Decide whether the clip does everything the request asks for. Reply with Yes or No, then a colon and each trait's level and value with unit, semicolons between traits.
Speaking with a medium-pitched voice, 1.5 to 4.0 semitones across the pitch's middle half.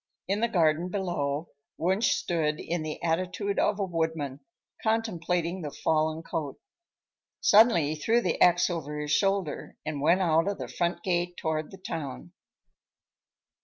Yes: medium, 170 Hz; average, 3.2 semitones